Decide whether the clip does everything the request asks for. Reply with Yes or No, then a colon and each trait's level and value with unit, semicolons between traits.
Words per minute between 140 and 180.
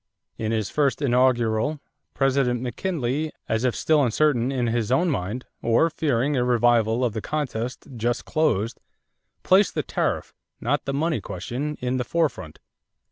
Yes: average, 150 wpm